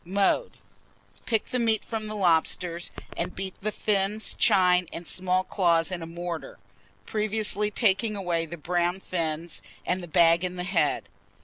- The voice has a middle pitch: Yes, medium, 180 Hz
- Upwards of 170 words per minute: No, average, 155 wpm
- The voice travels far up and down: No, average, 3.4 semitones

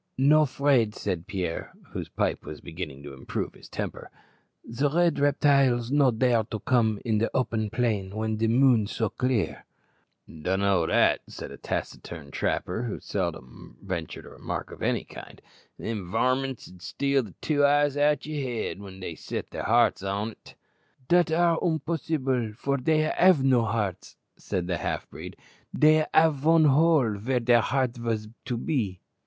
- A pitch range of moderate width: No, wide, 5.8 semitones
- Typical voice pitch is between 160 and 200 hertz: No, low, 120 Hz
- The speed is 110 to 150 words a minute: No, average, 165 wpm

